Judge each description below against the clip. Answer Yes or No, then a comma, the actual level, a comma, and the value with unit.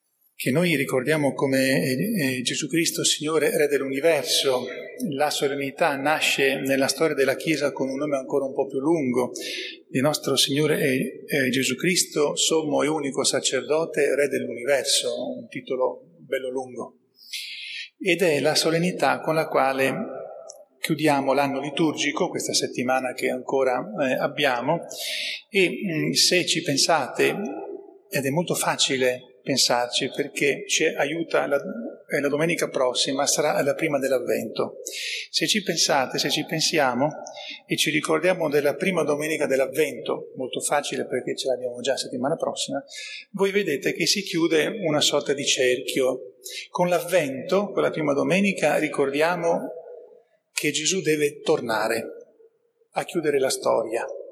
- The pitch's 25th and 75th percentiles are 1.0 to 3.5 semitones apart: No, average, 5.1 semitones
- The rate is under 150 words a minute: Yes, average, 135 wpm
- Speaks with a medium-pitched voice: Yes, medium, 155 Hz